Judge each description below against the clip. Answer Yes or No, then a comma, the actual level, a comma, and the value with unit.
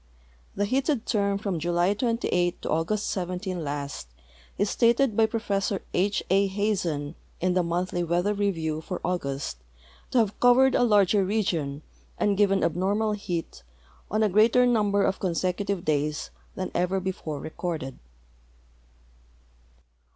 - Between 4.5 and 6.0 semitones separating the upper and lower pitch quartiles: No, average, 3.4 semitones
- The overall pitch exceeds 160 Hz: Yes, high, 190 Hz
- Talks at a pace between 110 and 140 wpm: Yes, slow, 135 wpm